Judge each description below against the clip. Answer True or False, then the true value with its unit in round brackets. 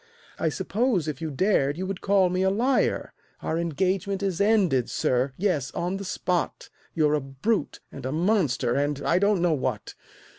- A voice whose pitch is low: False (175 Hz)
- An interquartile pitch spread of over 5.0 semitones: True (5.4 semitones)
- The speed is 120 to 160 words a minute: False (180 wpm)